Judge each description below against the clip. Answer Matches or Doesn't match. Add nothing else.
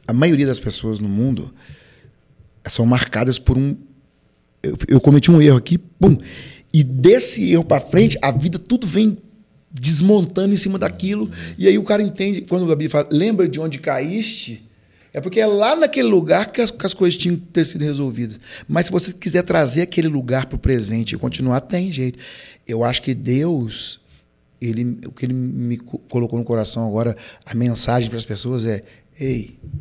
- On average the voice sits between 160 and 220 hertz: Doesn't match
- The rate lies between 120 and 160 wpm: Doesn't match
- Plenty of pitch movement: Matches